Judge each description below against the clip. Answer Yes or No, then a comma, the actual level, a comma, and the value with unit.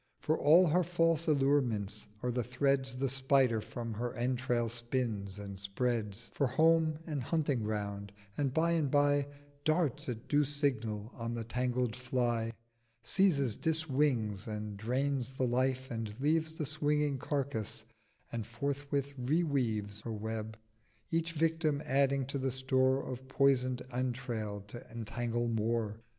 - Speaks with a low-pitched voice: Yes, low, 130 Hz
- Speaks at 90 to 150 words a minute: Yes, average, 145 wpm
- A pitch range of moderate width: Yes, average, 3.9 semitones